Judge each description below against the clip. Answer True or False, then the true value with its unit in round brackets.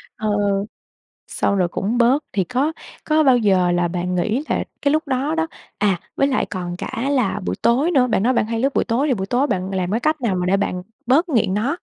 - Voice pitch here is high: True (230 Hz)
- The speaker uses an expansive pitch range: True (6.1 semitones)